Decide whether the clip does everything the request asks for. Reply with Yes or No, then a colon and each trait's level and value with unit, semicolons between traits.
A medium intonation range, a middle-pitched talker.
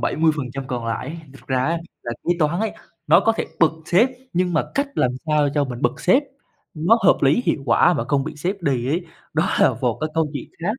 Yes: average, 4.3 semitones; medium, 155 Hz